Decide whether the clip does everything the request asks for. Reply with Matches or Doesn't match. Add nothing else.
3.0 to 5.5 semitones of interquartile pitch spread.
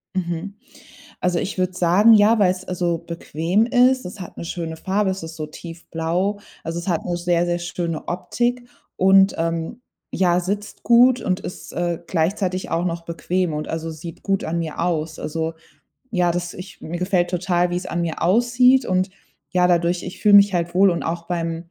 Doesn't match